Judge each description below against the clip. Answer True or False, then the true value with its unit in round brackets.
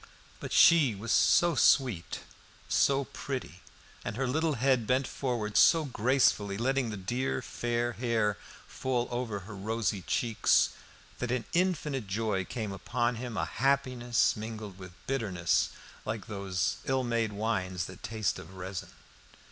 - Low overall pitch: True (115 Hz)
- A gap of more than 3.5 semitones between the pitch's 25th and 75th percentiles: True (4.3 semitones)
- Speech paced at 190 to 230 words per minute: False (140 wpm)